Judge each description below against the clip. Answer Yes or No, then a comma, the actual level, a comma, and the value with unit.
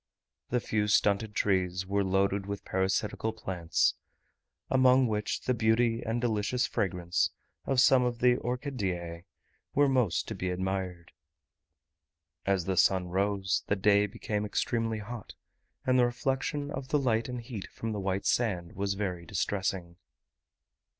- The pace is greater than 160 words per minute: No, average, 145 wpm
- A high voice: No, low, 105 Hz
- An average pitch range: Yes, average, 4.3 semitones